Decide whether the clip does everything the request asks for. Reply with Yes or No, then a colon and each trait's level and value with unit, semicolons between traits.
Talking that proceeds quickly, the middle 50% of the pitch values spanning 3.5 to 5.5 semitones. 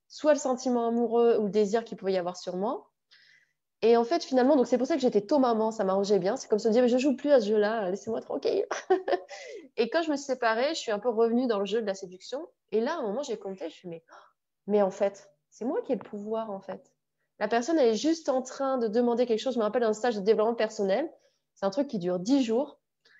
Yes: fast, 275 wpm; average, 4.0 semitones